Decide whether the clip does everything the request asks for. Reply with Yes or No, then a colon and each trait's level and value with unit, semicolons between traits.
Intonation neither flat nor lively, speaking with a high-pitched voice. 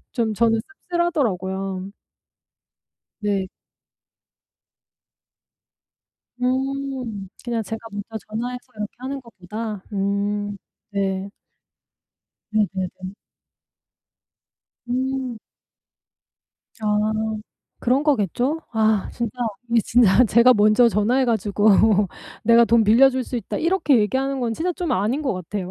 Yes: average, 3.9 semitones; high, 225 Hz